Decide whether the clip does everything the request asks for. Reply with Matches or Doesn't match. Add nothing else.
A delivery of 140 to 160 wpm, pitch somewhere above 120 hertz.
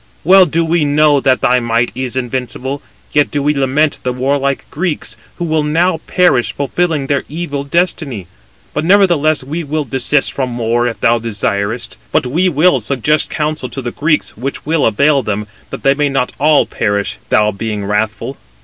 Doesn't match